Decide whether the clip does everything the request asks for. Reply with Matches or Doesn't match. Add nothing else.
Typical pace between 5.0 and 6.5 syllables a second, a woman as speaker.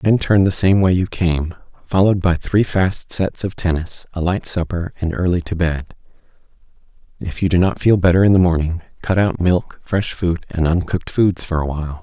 Doesn't match